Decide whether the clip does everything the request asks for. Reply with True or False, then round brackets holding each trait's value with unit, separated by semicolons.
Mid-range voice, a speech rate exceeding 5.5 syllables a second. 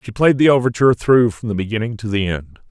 False (115 Hz; 6.4 syllables/s)